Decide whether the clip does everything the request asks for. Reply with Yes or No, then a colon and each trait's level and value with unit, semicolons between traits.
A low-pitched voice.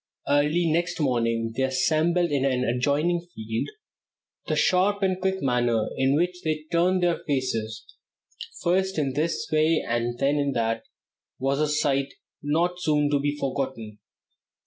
No: medium, 145 Hz